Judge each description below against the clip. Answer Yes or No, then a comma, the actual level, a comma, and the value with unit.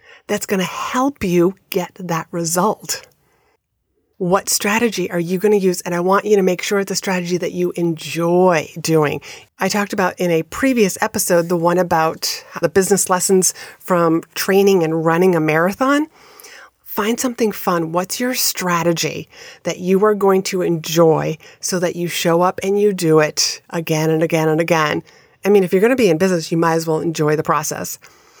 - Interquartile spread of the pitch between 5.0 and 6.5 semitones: No, average, 3.2 semitones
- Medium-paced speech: Yes, average, 185 wpm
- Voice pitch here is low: No, medium, 180 Hz